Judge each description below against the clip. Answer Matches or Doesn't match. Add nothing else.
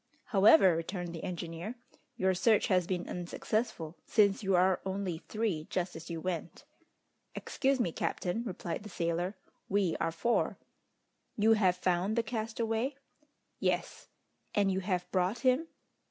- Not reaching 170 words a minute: Matches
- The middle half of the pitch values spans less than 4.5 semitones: Matches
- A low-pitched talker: Doesn't match